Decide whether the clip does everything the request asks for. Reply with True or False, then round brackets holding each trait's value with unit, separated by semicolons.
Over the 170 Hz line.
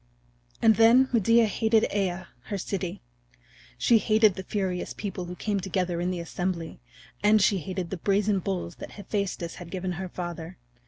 True (190 Hz)